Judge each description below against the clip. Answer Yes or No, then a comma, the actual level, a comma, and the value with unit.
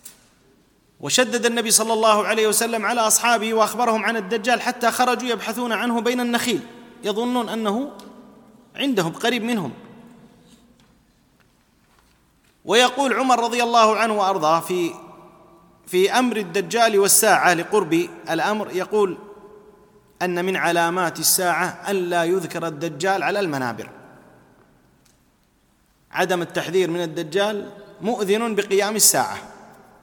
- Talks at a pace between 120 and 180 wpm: No, average, 105 wpm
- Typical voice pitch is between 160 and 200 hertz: No, high, 210 Hz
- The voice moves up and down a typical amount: Yes, average, 4.1 semitones